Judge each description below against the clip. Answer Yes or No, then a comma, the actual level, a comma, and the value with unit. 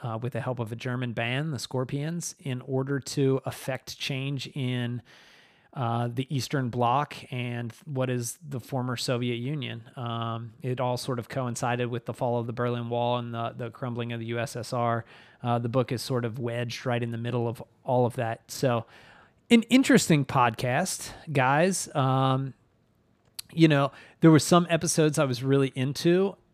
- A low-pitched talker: Yes, low, 125 Hz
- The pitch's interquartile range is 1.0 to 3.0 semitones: Yes, narrow, 2.5 semitones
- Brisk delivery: No, average, 175 wpm